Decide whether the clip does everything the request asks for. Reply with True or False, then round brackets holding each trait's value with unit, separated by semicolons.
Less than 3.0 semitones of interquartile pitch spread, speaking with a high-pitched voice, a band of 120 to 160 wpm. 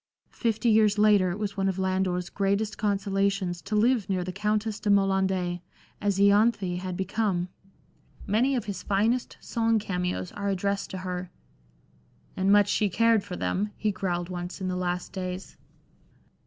False (2.4 semitones; 195 Hz; 170 wpm)